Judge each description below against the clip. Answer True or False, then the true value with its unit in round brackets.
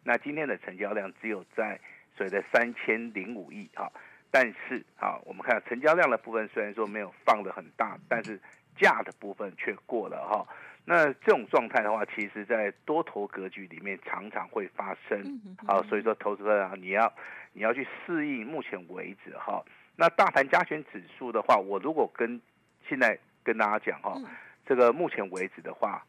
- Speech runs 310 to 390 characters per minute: False (275 characters per minute)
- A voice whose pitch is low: False (145 Hz)